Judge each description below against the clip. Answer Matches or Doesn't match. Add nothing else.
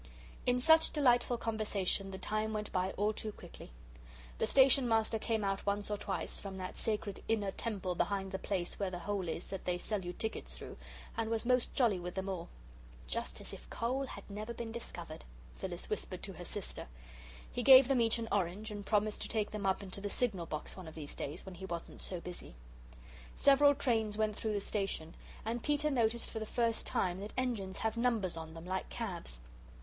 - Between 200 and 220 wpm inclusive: Matches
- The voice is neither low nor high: Doesn't match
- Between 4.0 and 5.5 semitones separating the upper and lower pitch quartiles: Doesn't match